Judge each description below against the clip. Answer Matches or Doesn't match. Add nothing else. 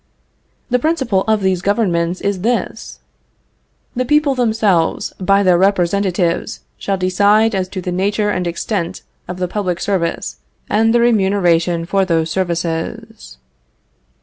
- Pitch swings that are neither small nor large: Matches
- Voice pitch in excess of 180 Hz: Matches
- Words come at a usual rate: Doesn't match